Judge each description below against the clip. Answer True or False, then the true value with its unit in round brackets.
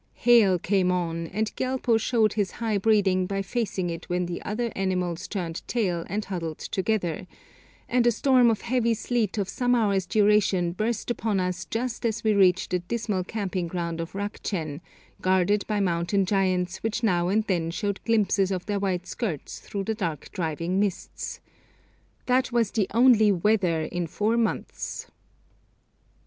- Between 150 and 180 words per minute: True (160 wpm)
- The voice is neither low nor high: False (195 Hz)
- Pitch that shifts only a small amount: False (3.7 semitones)